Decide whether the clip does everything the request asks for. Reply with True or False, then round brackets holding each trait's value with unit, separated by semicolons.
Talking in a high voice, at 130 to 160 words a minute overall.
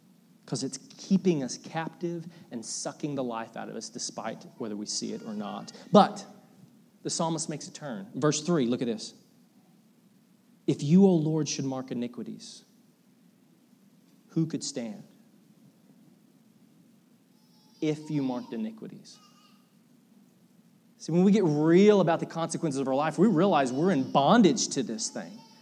True (210 Hz; 150 wpm)